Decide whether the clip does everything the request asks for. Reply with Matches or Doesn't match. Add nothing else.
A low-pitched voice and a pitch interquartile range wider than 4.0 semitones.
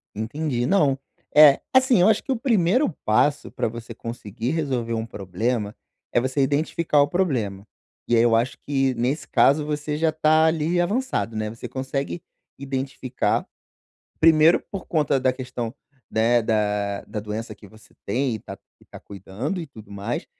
Matches